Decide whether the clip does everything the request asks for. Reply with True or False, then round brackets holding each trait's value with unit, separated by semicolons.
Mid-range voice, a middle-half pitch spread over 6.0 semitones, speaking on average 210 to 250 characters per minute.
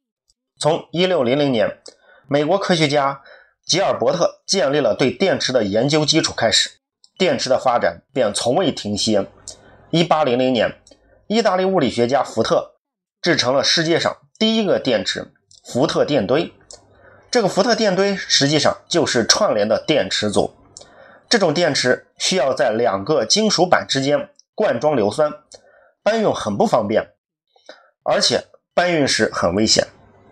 True (150 Hz; 7.0 semitones; 230 characters per minute)